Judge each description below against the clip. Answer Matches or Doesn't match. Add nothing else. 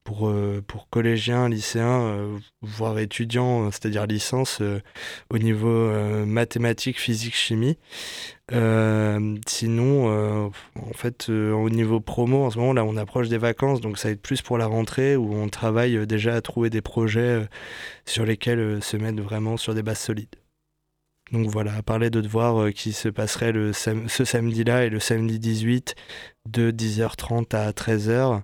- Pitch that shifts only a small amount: Matches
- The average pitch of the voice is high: Doesn't match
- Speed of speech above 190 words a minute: Doesn't match